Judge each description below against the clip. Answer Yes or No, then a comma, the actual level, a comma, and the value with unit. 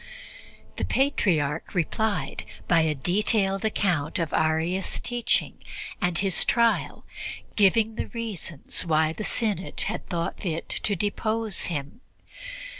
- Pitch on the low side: No, high, 190 Hz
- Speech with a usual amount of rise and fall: Yes, average, 4.9 semitones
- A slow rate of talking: Yes, slow, 115 wpm